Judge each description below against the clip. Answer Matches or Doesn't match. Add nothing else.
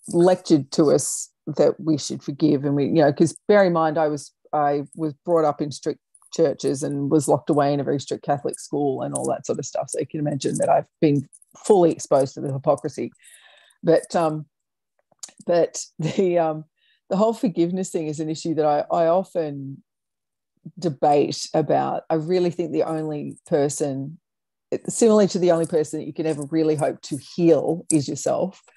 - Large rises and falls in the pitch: Doesn't match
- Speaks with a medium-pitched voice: Matches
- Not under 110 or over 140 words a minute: Doesn't match